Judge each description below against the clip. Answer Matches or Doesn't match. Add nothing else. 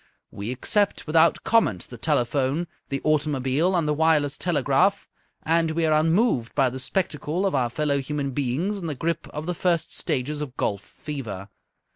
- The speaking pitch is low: Doesn't match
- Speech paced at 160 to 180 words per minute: Matches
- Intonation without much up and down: Doesn't match